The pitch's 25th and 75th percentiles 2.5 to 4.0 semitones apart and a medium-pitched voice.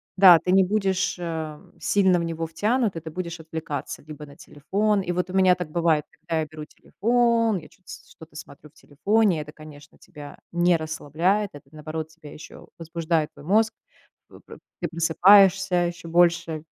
Yes: average, 3.4 semitones; medium, 170 Hz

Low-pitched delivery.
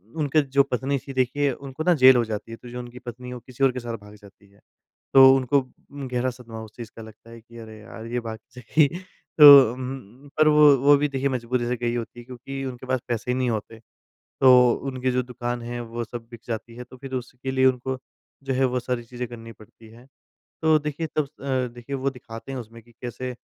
Yes: low, 125 Hz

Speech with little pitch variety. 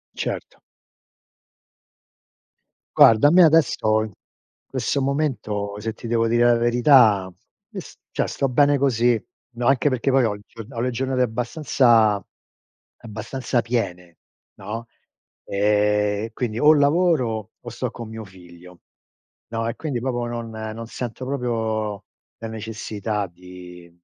No: average, 3.3 semitones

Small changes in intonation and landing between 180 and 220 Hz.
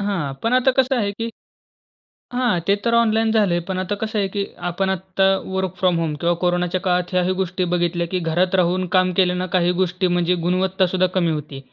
Yes: narrow, 2.0 semitones; medium, 185 Hz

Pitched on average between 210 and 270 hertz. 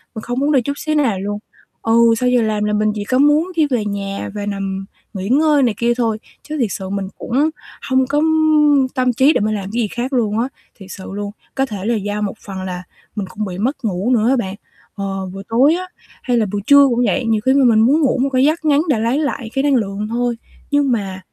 Yes: high, 230 Hz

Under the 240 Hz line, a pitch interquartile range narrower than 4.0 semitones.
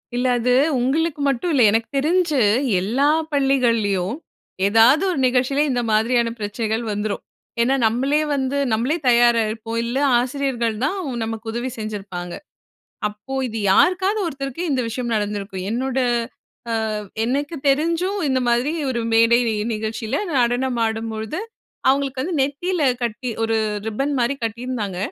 No: high, 245 Hz; average, 3.6 semitones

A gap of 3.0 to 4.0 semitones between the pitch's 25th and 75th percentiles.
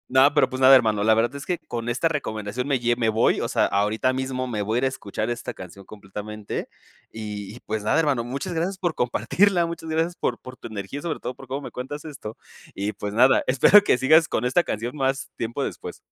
No: average, 4.7 semitones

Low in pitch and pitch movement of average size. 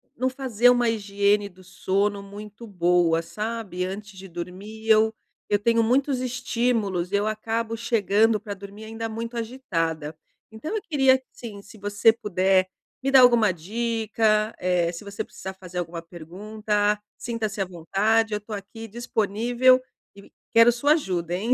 No: high, 210 Hz; average, 3.2 semitones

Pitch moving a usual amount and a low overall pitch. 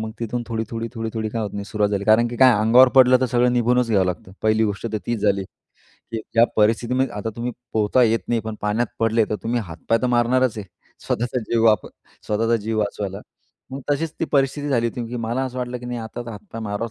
No: narrow, 2.2 semitones; low, 115 Hz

